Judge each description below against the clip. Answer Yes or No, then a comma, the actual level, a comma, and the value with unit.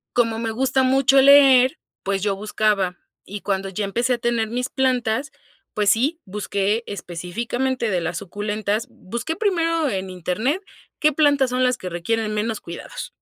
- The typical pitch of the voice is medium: No, high, 225 Hz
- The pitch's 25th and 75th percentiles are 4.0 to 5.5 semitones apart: Yes, average, 4.7 semitones